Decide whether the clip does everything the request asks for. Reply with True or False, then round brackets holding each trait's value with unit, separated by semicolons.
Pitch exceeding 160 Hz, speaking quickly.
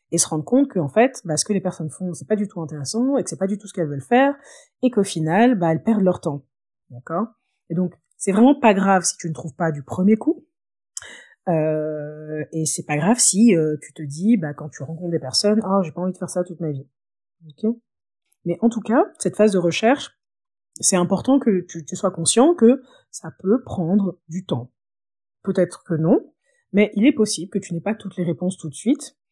True (185 Hz; 235 wpm)